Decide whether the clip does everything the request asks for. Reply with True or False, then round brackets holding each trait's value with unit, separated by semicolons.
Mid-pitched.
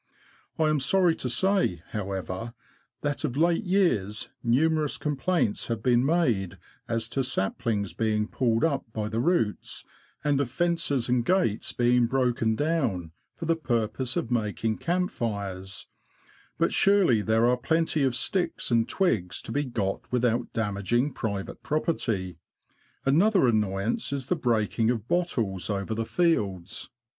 False (120 Hz)